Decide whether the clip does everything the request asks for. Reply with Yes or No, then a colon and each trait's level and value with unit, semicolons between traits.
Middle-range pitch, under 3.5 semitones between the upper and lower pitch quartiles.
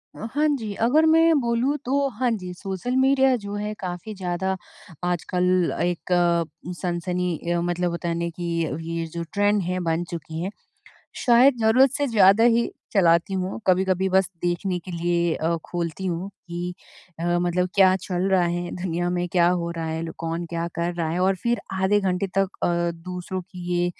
Yes: medium, 180 Hz; average, 2.9 semitones